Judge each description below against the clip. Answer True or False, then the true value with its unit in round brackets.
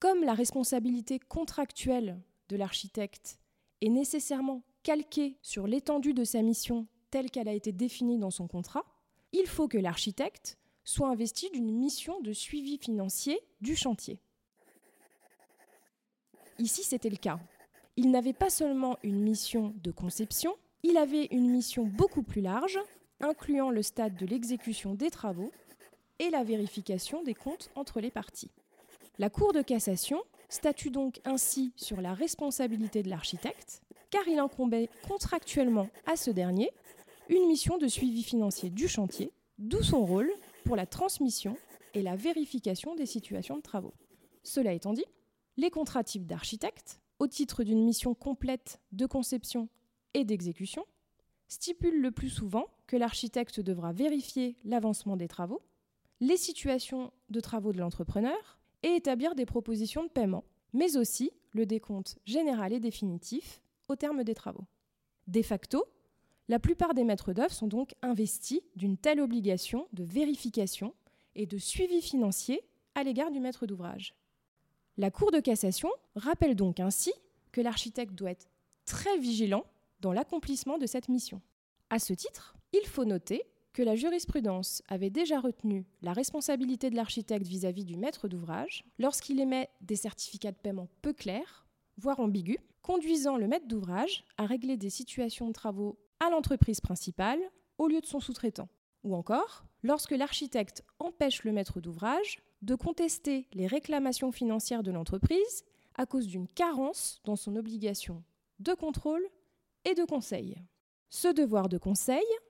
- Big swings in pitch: True (6.0 semitones)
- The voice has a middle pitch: False (245 Hz)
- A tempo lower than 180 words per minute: True (150 wpm)